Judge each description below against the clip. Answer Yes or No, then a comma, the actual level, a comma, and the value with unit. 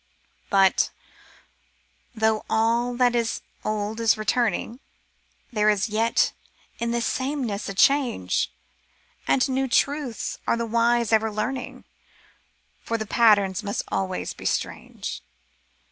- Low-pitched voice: No, high, 230 Hz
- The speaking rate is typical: No, slow, 120 wpm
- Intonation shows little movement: Yes, narrow, 2.2 semitones